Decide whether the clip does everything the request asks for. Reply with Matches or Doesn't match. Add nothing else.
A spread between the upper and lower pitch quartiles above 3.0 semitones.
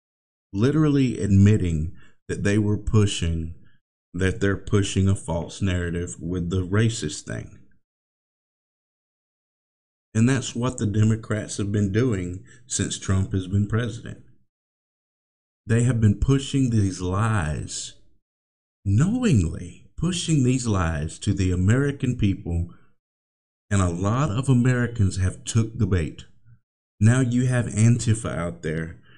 Matches